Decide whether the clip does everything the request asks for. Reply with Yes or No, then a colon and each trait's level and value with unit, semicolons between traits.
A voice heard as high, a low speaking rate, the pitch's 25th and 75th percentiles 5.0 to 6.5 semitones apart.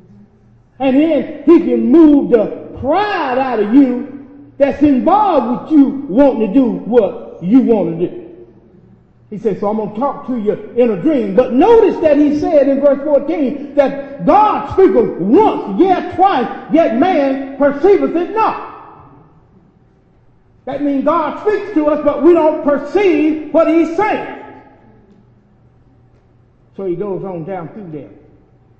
No: very high, 280 Hz; average, 150 wpm; average, 5.3 semitones